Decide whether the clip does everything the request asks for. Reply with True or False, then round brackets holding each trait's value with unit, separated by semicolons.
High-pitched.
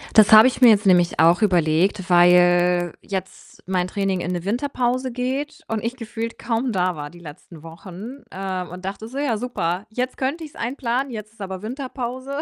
True (210 Hz)